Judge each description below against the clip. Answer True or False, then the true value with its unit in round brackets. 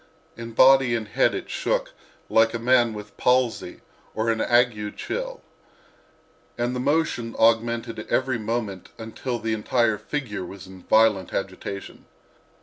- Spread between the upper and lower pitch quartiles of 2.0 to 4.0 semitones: True (2.4 semitones)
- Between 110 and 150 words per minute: True (140 wpm)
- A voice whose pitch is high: False (115 Hz)